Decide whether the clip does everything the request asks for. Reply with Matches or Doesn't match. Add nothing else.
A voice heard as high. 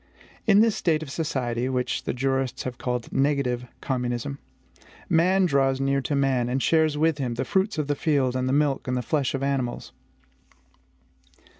Doesn't match